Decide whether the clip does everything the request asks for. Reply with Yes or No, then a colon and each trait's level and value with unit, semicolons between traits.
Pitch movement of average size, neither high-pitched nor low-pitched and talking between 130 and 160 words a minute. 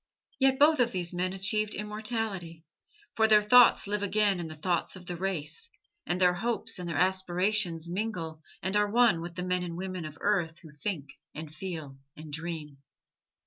No: average, 4.1 semitones; medium, 180 Hz; average, 185 wpm